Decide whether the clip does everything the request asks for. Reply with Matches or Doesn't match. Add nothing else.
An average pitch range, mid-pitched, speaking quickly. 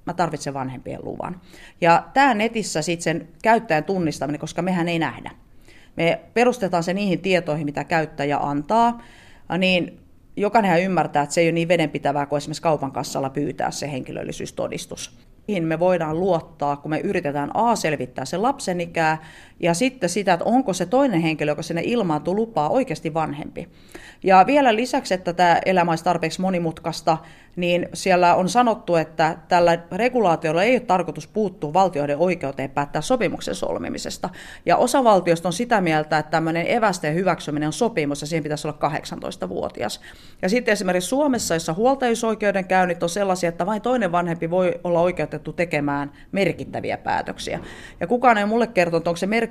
Matches